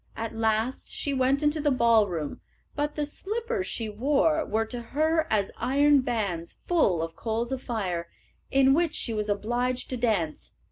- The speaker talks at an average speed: Yes, average, 170 wpm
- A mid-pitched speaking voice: No, high, 245 Hz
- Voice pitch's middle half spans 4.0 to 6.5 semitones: Yes, average, 5.2 semitones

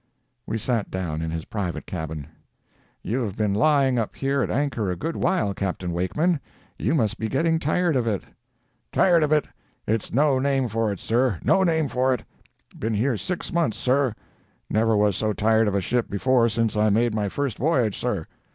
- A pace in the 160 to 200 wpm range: Yes, average, 190 wpm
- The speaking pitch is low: Yes, low, 115 Hz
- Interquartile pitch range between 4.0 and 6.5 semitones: Yes, average, 5.2 semitones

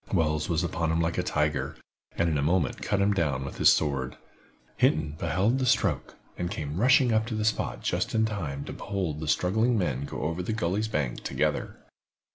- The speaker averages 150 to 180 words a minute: No, fast, 205 wpm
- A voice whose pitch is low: Yes, very low, 85 Hz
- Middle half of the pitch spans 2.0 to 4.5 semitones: No, wide, 5.6 semitones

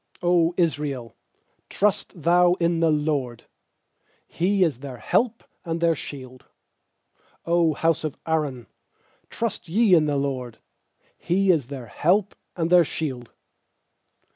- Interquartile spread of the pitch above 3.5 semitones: Yes, average, 4.0 semitones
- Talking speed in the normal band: No, slow, 125 wpm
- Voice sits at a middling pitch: Yes, medium, 165 Hz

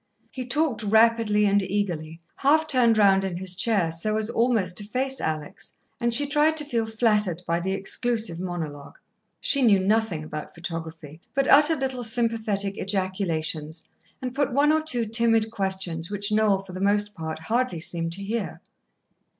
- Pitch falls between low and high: No, high, 205 Hz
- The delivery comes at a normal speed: Yes, average, 165 wpm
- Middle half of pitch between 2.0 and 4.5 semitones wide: No, average, 4.9 semitones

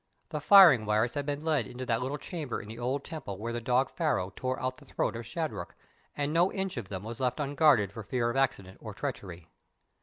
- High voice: No, low, 130 Hz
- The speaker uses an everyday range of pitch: Yes, average, 4.7 semitones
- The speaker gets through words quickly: Yes, fast, 230 wpm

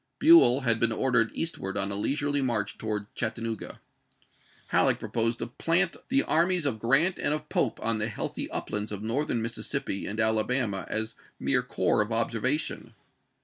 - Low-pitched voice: Yes, low, 115 Hz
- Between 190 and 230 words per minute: No, average, 160 wpm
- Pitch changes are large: No, average, 4.5 semitones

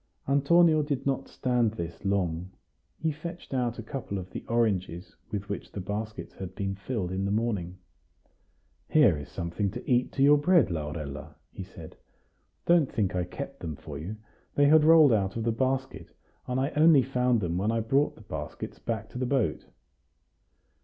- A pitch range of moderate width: No, wide, 6.5 semitones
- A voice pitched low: Yes, low, 115 Hz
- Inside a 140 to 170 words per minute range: No, average, 180 wpm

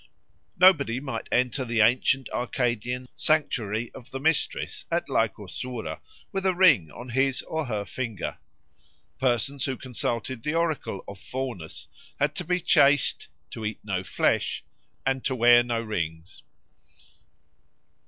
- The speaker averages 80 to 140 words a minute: Yes, slow, 135 wpm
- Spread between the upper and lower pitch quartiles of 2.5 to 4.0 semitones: Yes, average, 3.7 semitones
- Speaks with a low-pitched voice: Yes, low, 125 Hz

